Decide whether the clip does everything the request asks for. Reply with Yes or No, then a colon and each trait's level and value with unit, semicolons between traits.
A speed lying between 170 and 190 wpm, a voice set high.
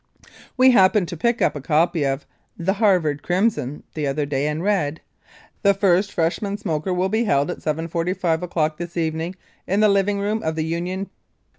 No: average, 180 wpm; medium, 175 Hz